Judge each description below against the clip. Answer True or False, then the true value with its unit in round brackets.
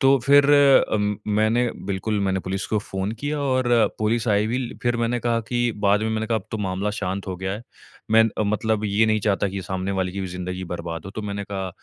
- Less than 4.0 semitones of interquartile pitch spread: True (2.9 semitones)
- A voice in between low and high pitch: False (105 Hz)